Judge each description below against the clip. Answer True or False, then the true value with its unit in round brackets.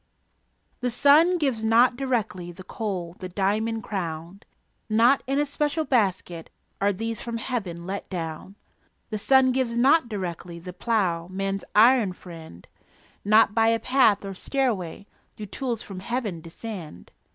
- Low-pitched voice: False (215 Hz)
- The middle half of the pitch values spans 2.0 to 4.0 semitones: False (5.1 semitones)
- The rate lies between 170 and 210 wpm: False (145 wpm)